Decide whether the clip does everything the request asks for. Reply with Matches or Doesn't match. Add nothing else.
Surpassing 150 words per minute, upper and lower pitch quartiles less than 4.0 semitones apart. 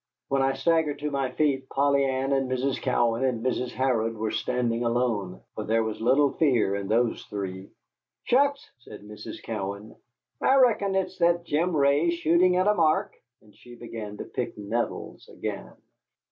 Doesn't match